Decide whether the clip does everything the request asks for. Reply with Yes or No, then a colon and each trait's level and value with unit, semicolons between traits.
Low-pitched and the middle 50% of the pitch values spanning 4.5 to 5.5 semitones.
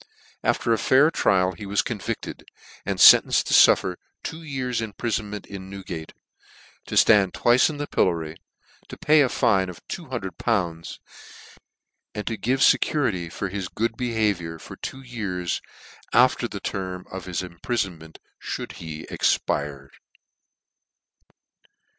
Yes: low, 100 Hz; average, 5.1 semitones